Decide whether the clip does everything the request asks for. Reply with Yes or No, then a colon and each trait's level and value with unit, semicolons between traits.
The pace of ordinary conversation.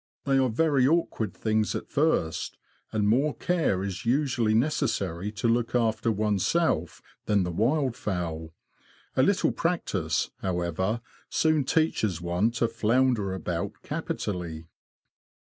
No: slow, 125 wpm